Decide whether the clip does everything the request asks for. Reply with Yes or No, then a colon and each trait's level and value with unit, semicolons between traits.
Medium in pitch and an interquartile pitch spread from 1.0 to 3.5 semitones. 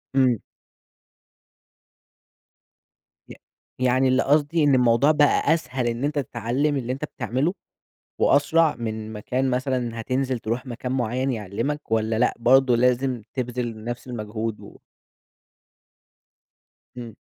No: low, 125 Hz; average, 2.7 semitones